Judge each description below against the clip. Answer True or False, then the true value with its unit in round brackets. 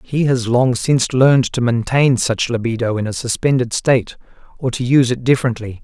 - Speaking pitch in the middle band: False (125 Hz)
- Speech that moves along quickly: False (185 wpm)